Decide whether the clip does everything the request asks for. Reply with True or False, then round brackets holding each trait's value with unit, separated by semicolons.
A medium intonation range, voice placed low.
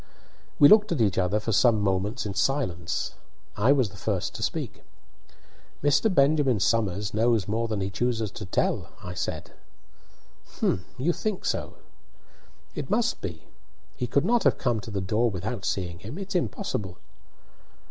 False (5.8 semitones; 110 Hz)